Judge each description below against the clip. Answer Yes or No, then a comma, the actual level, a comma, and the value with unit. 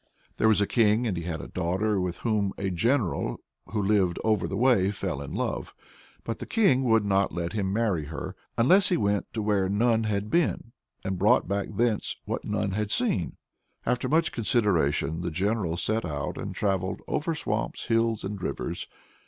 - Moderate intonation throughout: Yes, average, 3.5 semitones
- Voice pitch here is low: Yes, low, 105 Hz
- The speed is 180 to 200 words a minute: Yes, average, 185 wpm